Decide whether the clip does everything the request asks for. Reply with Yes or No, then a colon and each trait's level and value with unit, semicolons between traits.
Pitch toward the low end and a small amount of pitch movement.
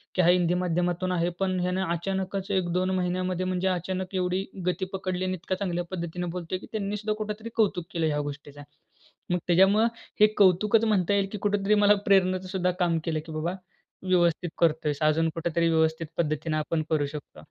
No: medium, 180 Hz; narrow, 2.3 semitones